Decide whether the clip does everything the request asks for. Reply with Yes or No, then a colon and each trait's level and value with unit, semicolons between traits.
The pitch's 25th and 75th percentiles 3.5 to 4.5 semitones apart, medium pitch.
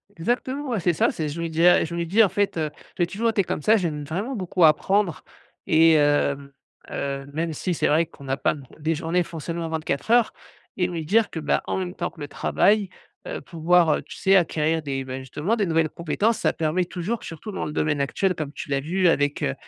Yes: average, 3.9 semitones; medium, 165 Hz